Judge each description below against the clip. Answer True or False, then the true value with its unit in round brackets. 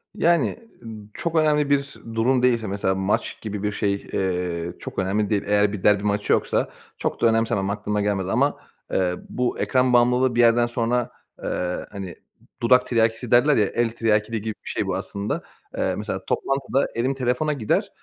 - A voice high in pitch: False (115 Hz)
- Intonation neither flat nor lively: True (3.6 semitones)